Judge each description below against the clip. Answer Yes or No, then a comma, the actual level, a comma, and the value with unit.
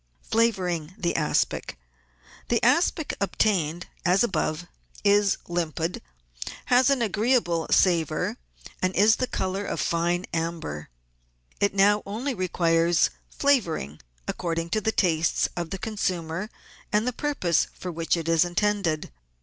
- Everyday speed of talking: No, slow, 130 wpm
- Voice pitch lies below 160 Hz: No, medium, 180 Hz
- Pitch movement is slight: No, average, 4.1 semitones